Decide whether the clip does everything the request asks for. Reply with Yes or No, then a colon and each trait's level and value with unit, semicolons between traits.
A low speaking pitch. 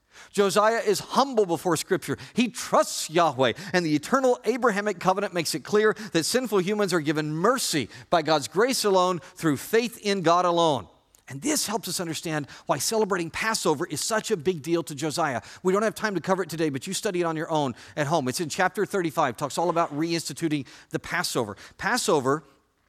No: medium, 175 Hz